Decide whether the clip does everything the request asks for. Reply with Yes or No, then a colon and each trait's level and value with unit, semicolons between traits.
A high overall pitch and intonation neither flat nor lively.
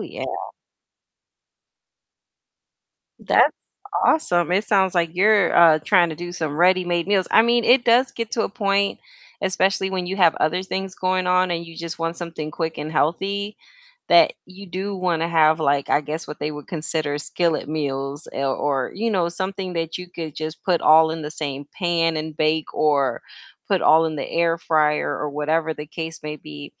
No: medium, 165 Hz; average, 3.3 semitones